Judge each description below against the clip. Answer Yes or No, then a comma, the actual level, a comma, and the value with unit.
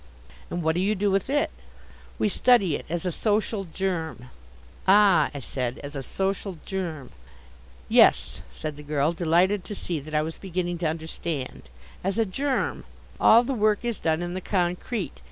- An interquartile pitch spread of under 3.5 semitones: No, average, 4.3 semitones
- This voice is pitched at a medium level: Yes, medium, 180 Hz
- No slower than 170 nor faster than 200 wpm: Yes, average, 175 wpm